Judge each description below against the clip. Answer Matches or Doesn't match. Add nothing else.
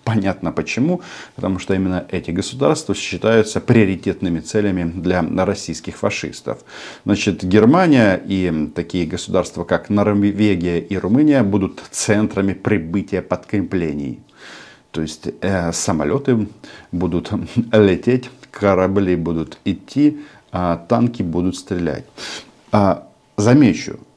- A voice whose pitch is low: Matches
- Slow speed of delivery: Matches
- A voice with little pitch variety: Doesn't match